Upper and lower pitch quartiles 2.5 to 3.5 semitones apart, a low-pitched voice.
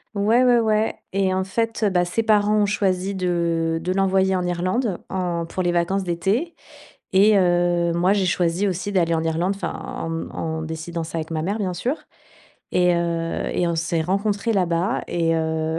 No: average, 2.9 semitones; medium, 180 Hz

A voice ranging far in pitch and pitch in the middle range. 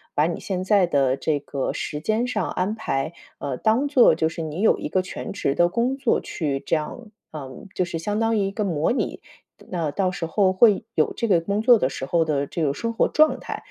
Yes: wide, 6.1 semitones; medium, 180 Hz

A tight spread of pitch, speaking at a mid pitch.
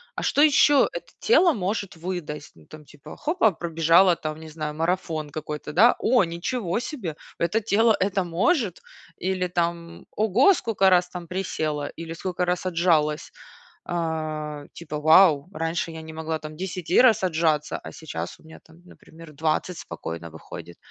No: average, 3.4 semitones; medium, 170 Hz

